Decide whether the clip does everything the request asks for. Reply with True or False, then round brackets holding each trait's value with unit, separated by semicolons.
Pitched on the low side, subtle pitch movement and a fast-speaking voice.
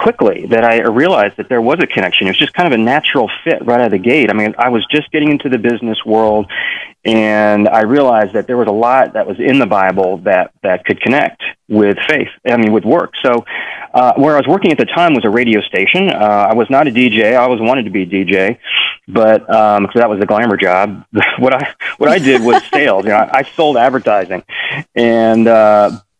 True (110 Hz; 2.3 semitones; 235 wpm)